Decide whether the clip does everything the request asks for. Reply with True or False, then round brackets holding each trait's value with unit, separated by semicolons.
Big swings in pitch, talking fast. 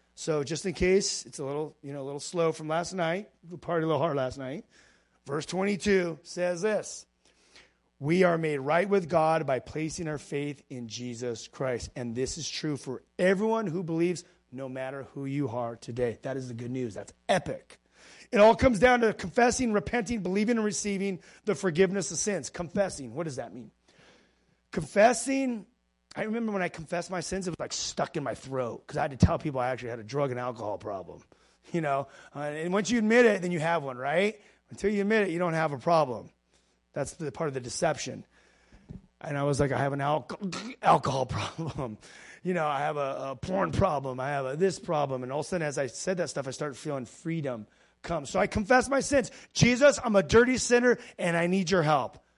True (6.0 semitones; 215 wpm)